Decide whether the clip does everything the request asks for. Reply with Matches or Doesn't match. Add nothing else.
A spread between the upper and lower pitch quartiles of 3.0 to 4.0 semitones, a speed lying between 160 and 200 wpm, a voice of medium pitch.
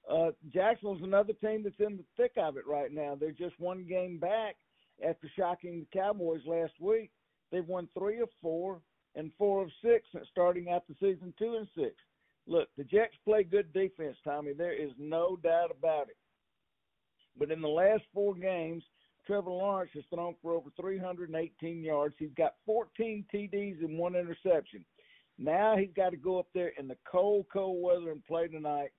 Matches